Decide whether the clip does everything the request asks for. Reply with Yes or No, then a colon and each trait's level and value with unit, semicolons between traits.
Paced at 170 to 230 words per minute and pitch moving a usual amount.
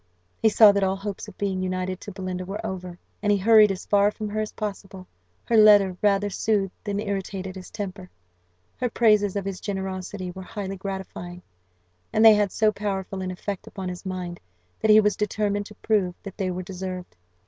No: average, 195 wpm; narrow, 1.9 semitones